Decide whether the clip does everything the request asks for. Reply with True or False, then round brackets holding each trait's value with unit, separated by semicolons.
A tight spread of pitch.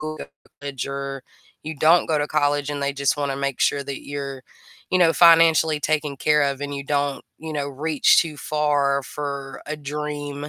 True (1.5 semitones)